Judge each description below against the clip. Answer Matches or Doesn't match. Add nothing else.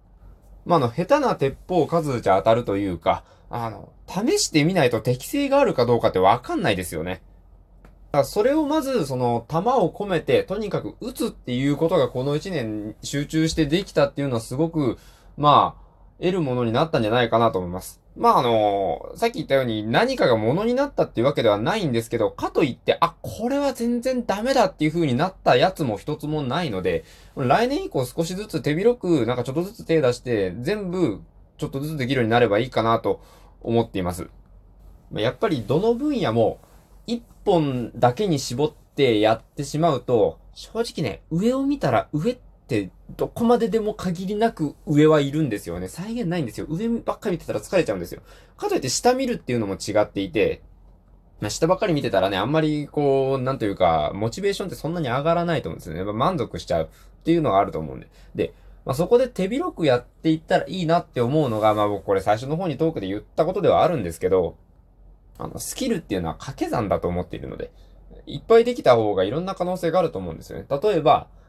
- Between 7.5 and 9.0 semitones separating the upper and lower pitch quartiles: Matches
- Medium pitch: Matches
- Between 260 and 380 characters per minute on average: Doesn't match